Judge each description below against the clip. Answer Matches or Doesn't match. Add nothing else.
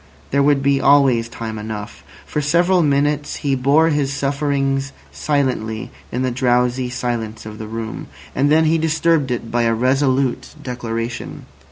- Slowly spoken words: Doesn't match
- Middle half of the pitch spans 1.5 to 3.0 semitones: Doesn't match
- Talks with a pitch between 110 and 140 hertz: Matches